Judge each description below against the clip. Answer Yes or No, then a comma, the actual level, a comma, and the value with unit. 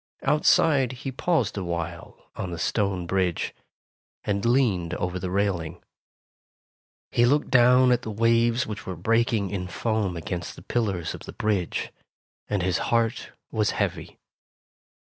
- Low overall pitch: Yes, low, 105 Hz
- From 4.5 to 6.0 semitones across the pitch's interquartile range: Yes, average, 4.8 semitones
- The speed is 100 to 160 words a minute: Yes, average, 140 wpm